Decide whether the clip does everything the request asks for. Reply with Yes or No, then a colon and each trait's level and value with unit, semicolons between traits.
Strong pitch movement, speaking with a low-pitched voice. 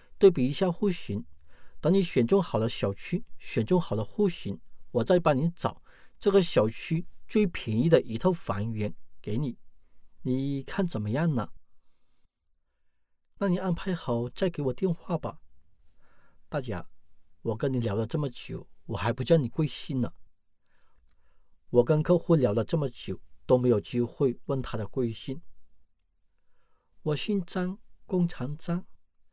Yes: wide, 9.0 semitones; low, 125 Hz